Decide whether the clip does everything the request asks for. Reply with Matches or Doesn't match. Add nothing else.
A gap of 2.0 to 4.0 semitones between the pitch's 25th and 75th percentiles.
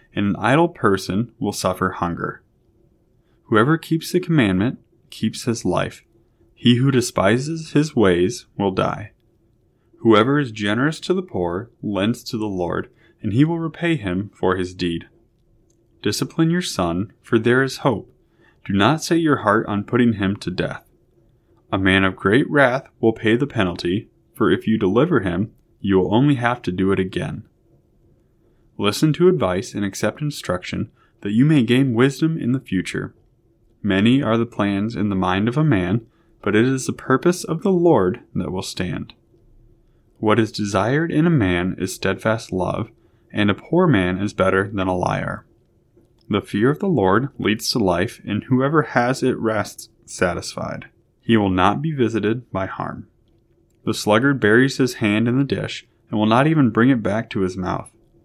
Doesn't match